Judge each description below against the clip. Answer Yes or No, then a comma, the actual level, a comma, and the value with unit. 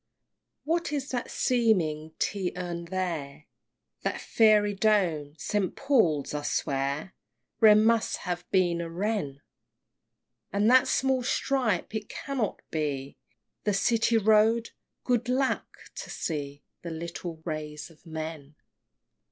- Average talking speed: No, slow, 125 wpm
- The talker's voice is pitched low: No, medium, 185 Hz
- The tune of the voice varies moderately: No, wide, 6.3 semitones